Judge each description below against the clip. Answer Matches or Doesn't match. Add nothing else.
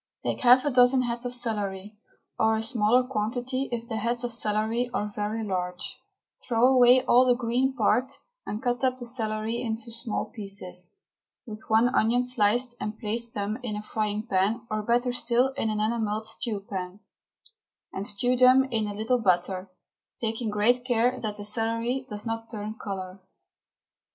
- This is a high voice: Matches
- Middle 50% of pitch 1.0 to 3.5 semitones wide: Matches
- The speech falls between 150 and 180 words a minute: Matches